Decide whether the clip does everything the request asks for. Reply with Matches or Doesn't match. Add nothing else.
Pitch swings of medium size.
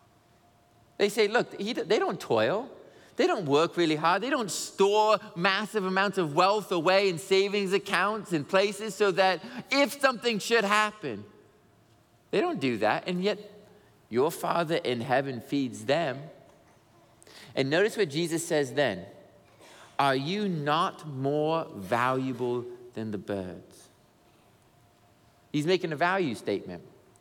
Doesn't match